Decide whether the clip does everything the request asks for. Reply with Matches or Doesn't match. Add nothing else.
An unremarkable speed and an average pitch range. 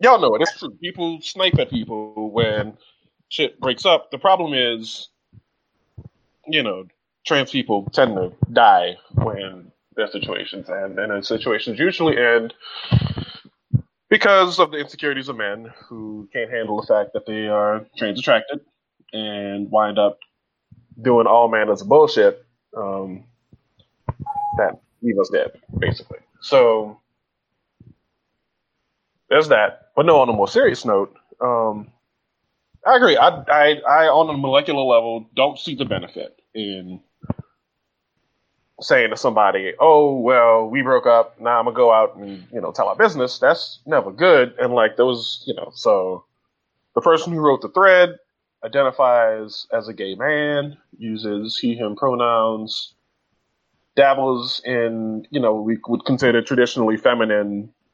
Doesn't match